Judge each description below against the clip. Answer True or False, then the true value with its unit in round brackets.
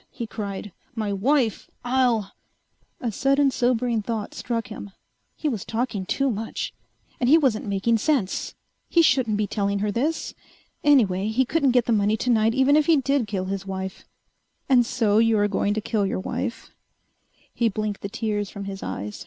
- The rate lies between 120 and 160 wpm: False (180 wpm)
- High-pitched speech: True (225 Hz)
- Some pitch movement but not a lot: True (3.9 semitones)